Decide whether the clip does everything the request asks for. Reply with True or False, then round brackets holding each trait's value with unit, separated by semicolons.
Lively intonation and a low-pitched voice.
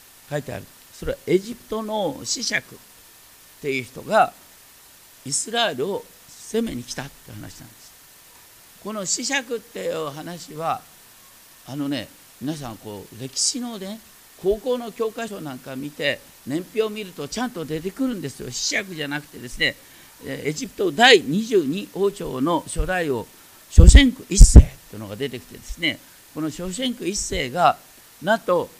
False (8.9 semitones; 185 Hz)